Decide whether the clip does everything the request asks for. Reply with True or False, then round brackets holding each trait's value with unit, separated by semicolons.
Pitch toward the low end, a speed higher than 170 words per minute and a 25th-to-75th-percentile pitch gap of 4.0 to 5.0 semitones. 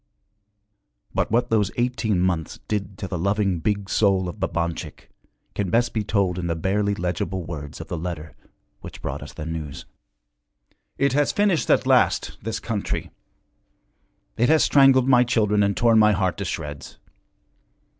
False (100 Hz; 165 wpm; 4.4 semitones)